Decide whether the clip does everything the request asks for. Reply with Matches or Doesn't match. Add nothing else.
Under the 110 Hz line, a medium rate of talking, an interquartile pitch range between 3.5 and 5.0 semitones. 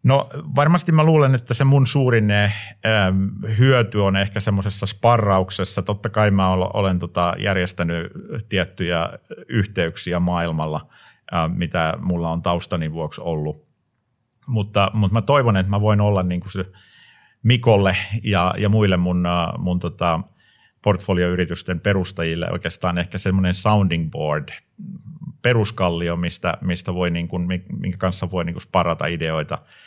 Matches